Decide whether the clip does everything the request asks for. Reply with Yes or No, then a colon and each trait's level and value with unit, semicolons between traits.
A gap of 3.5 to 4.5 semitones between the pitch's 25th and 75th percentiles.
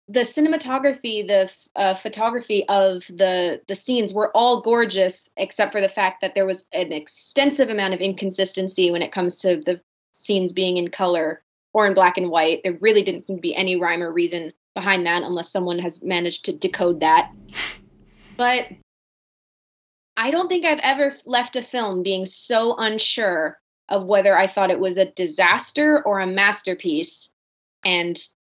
Yes: average, 3.8 semitones